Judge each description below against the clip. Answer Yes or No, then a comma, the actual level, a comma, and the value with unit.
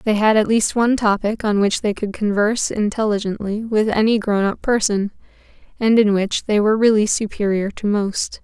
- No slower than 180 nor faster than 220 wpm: Yes, average, 185 wpm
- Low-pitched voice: No, high, 210 Hz